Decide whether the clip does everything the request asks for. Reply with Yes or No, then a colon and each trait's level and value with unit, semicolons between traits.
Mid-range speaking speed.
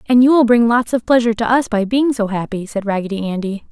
No: fast, 260 wpm